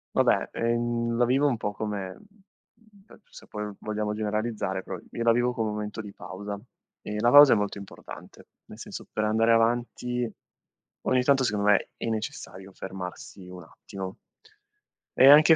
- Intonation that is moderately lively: Yes, average, 3.0 semitones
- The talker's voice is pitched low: Yes, low, 110 Hz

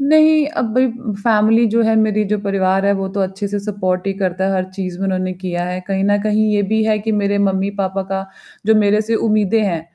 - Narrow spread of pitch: Yes, narrow, 2.1 semitones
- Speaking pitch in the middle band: No, high, 200 Hz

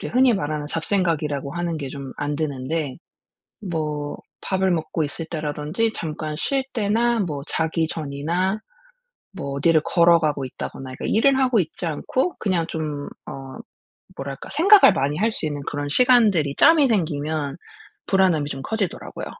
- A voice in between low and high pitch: Yes, medium, 160 Hz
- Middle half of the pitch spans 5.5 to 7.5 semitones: No, average, 5.1 semitones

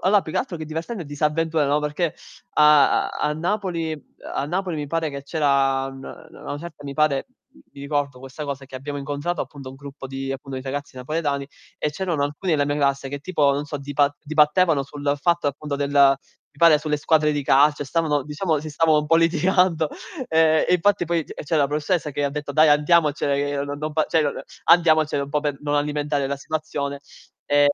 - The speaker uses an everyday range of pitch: No, narrow, 2.0 semitones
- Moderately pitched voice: Yes, medium, 150 Hz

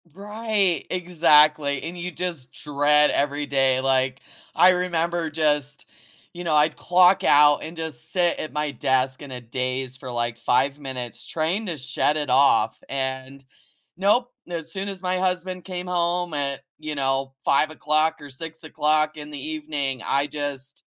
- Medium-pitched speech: Yes, medium, 150 Hz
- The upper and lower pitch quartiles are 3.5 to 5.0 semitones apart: Yes, average, 4.2 semitones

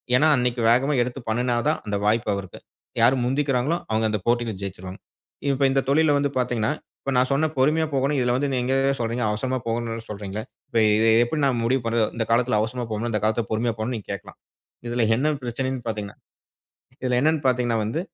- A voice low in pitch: Yes, low, 120 Hz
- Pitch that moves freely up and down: No, average, 3.0 semitones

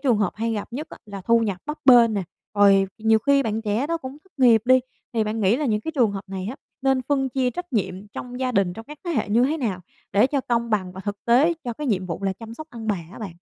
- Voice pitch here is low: No, high, 230 Hz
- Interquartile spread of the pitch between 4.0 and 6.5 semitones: Yes, average, 4.3 semitones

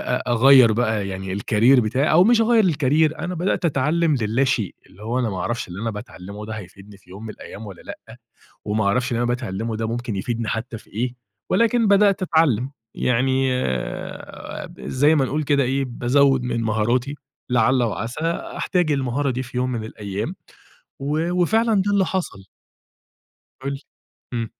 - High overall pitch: No, low, 125 Hz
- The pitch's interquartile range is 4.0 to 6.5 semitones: Yes, average, 5.2 semitones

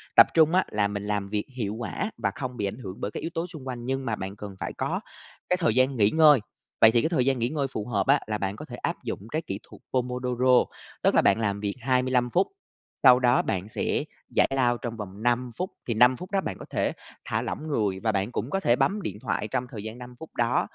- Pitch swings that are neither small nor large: Yes, average, 4.2 semitones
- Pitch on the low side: Yes, low, 120 Hz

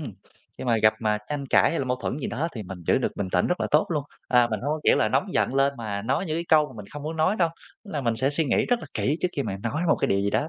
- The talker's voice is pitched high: No, low, 135 Hz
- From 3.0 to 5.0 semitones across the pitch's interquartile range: No, wide, 5.6 semitones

